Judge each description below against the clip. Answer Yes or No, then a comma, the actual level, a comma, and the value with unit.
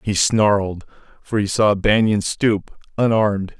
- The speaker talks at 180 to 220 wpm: No, slow, 135 wpm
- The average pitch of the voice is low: Yes, low, 105 Hz